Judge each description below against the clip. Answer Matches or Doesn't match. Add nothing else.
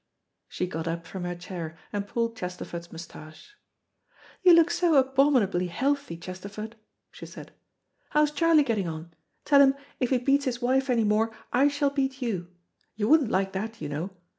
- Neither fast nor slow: Matches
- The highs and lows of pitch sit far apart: Matches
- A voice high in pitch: Matches